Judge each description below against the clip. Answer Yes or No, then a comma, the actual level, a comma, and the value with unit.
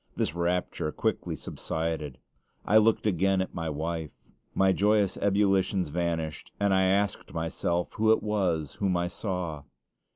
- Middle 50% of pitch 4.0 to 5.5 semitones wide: No, average, 3.3 semitones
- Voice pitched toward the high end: No, very low, 90 Hz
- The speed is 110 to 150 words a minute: Yes, average, 140 wpm